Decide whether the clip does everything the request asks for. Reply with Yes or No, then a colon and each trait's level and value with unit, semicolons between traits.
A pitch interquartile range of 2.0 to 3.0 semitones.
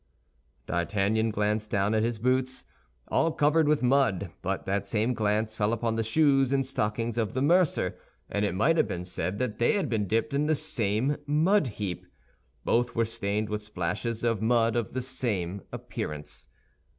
No: average, 3.9 semitones